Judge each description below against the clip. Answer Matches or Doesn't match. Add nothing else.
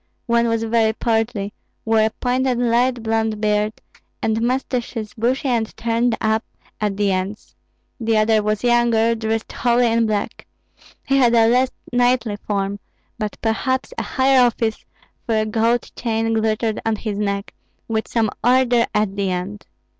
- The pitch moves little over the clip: Matches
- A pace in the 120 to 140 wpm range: Doesn't match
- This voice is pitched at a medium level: Doesn't match